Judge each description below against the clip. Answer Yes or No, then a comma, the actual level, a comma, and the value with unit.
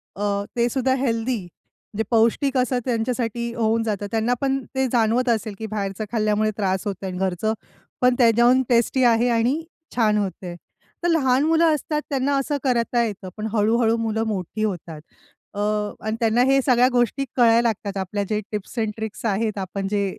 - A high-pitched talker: Yes, high, 225 Hz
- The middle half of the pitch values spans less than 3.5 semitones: Yes, average, 3.1 semitones